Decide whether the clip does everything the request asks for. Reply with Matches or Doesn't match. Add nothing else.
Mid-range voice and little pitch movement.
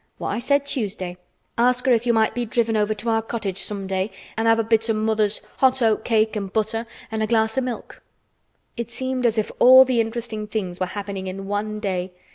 Doesn't match